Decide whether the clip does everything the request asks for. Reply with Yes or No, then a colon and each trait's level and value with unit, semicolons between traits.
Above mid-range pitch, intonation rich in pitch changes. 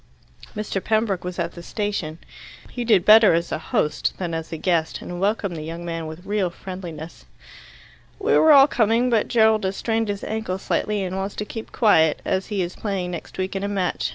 No: high, 195 Hz; average, 4.0 semitones